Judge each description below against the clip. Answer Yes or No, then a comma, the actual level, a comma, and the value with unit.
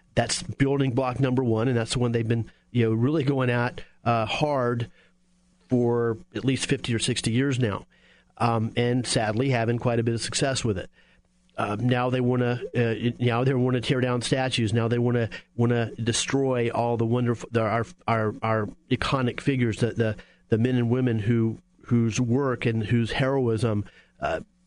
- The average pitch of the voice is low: Yes, low, 120 Hz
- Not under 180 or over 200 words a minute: Yes, average, 190 wpm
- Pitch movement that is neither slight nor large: No, narrow, 1.9 semitones